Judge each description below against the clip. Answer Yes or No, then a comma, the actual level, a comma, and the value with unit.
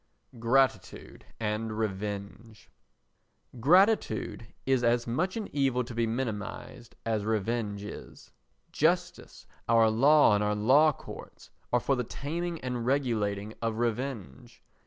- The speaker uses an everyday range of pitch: Yes, average, 4.0 semitones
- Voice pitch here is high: No, low, 115 Hz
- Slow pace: Yes, slow, 120 wpm